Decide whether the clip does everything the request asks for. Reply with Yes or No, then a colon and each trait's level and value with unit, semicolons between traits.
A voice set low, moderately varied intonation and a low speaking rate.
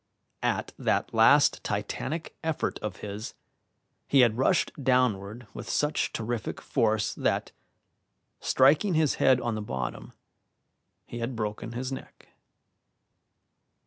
Yes: low, 120 Hz; average, 3.7 semitones; slow, 115 wpm